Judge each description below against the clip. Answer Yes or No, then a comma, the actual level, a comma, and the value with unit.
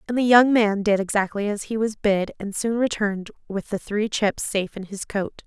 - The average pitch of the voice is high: Yes, high, 210 Hz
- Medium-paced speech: No, fast, 230 wpm